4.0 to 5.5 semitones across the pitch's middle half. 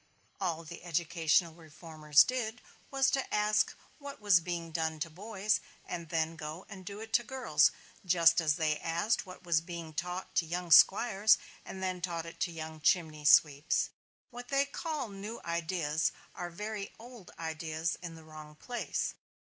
Yes: average, 4.3 semitones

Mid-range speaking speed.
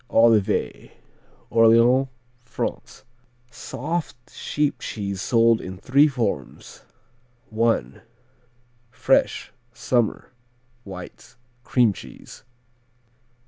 No: slow, 70 wpm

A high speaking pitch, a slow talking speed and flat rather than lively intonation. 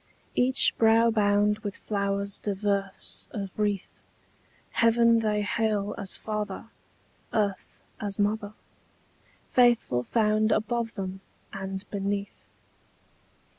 Yes: high, 210 Hz; slow, 95 wpm; narrow, 1.8 semitones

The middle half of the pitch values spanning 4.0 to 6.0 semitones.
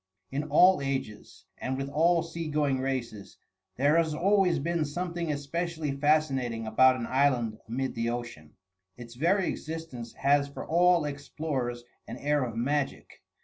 Yes: average, 4.5 semitones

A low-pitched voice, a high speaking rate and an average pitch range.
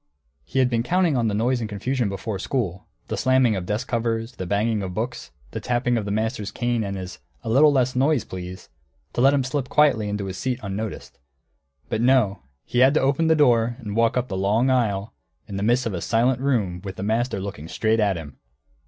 Yes: low, 115 Hz; fast, 225 wpm; average, 4.1 semitones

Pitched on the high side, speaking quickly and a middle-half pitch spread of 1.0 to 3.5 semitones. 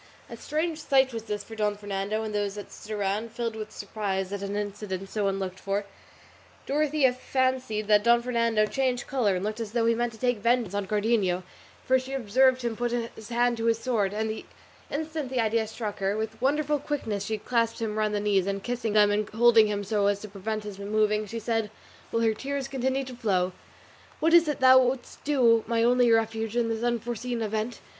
Yes: high, 225 Hz; fast, 210 wpm; average, 2.9 semitones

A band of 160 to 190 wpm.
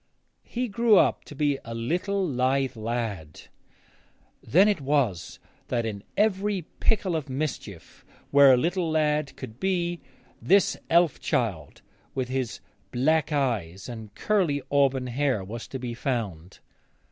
No: slow, 135 wpm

